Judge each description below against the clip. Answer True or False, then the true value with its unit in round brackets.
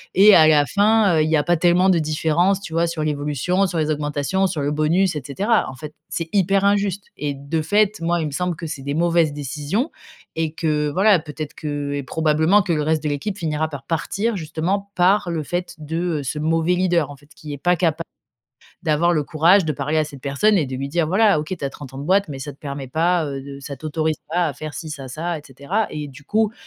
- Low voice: False (160 Hz)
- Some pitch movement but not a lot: True (3.5 semitones)